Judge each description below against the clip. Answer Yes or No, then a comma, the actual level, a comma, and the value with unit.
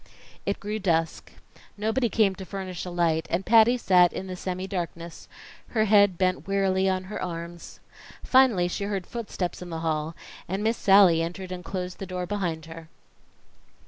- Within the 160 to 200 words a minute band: Yes, average, 175 wpm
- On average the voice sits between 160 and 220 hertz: Yes, medium, 185 Hz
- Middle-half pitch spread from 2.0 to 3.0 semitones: Yes, average, 2.7 semitones